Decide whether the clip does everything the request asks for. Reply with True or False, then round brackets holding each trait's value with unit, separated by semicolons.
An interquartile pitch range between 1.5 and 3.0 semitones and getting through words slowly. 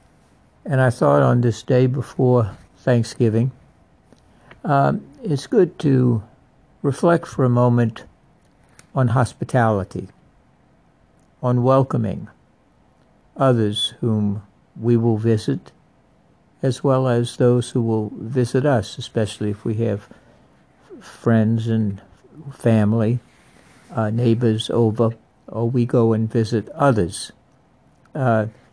True (2.5 semitones; 100 wpm)